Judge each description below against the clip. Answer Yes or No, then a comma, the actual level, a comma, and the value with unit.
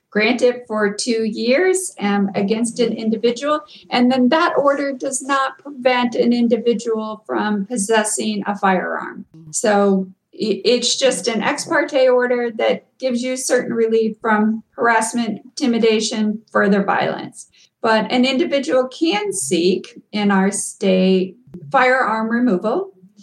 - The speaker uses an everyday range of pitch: Yes, average, 3.7 semitones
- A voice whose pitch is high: Yes, high, 230 Hz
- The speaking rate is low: Yes, slow, 125 wpm